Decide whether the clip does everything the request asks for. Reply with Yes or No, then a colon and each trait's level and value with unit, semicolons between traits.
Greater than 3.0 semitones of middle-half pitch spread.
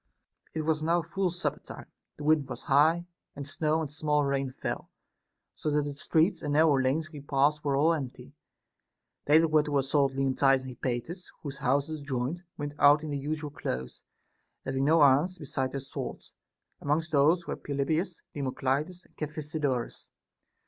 No: narrow, 2.4 semitones